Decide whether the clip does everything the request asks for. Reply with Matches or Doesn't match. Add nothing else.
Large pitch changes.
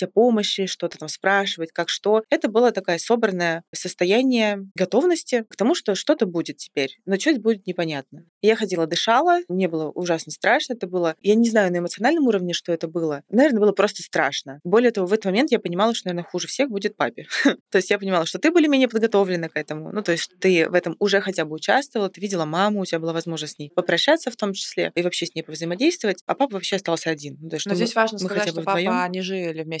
Doesn't match